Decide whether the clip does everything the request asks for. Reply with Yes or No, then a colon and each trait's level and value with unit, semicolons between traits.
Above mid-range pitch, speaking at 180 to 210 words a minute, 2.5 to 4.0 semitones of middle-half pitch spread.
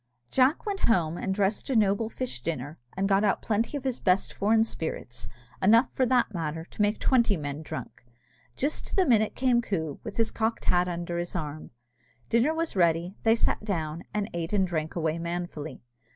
No: high, 195 Hz; average, 195 wpm; wide, 5.6 semitones